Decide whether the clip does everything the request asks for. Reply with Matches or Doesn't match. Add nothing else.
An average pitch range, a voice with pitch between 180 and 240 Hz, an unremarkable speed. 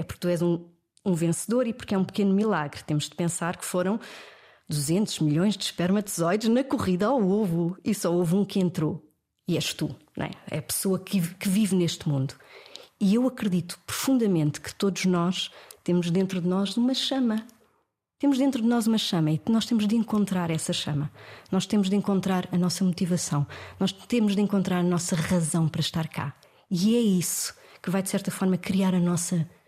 Doesn't match